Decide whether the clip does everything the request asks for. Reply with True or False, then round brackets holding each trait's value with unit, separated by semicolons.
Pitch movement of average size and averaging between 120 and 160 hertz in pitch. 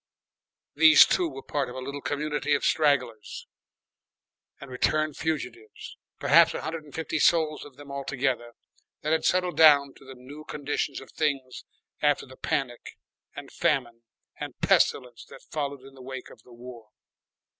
True (3.0 semitones; 140 Hz)